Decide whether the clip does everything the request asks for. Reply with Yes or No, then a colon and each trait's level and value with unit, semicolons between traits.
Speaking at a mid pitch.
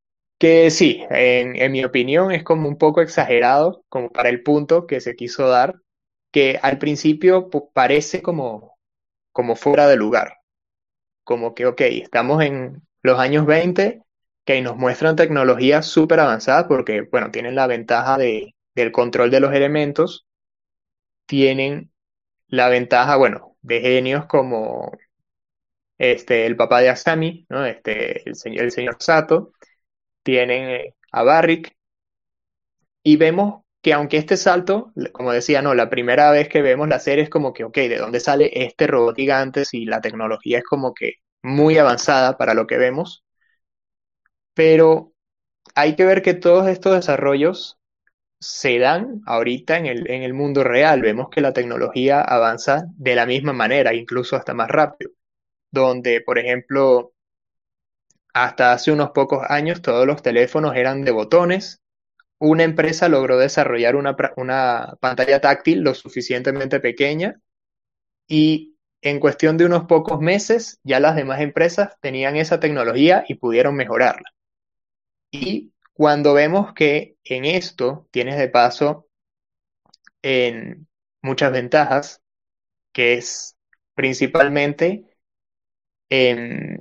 Yes: medium, 145 Hz